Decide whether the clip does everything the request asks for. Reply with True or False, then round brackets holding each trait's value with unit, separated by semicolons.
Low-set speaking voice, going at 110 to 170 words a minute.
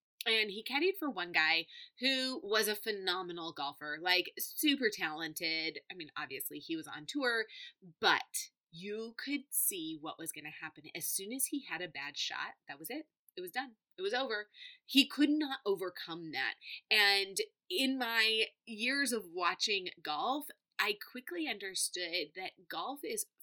False (230 Hz; 165 wpm)